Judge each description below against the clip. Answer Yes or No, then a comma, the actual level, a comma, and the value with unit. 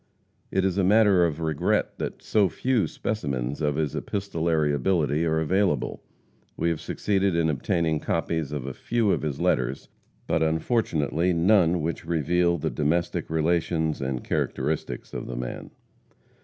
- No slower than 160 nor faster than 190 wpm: No, average, 150 wpm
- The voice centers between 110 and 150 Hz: No, very low, 80 Hz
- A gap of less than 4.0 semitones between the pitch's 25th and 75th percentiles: Yes, average, 3.5 semitones